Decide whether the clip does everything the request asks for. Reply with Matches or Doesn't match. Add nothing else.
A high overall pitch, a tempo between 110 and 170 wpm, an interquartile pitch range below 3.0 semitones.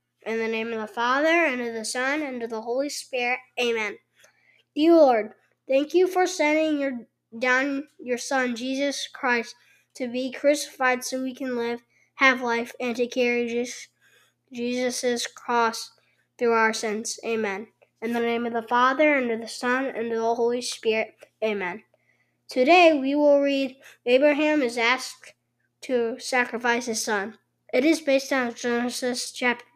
Matches